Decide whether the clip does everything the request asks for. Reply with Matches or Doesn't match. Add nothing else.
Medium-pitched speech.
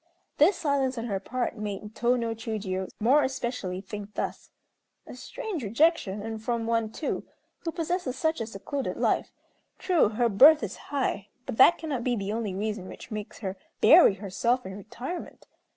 Doesn't match